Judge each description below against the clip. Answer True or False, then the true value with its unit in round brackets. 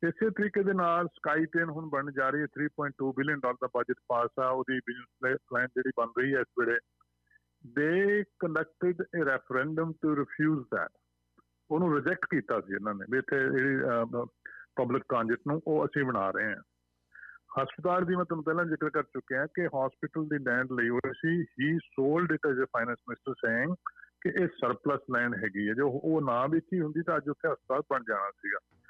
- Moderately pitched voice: True (145 Hz)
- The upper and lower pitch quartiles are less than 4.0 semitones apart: False (4.7 semitones)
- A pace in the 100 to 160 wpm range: False (190 wpm)